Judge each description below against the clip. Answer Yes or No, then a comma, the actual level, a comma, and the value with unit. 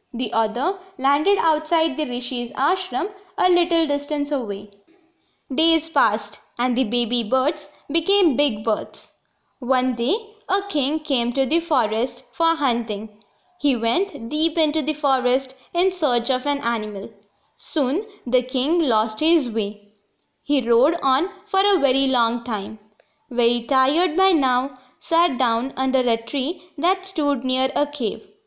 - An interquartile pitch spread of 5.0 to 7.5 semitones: Yes, wide, 5.4 semitones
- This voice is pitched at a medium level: No, very high, 275 Hz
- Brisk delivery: Yes, fast, 145 wpm